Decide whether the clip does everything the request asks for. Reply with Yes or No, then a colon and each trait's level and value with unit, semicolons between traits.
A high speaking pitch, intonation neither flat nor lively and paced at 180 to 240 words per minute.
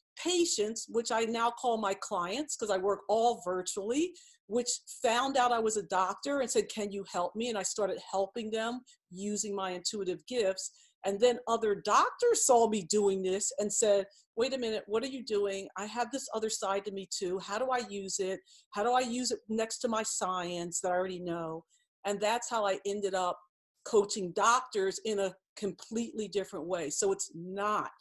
Yes: high, 210 Hz; average, 3.4 semitones; average, 200 wpm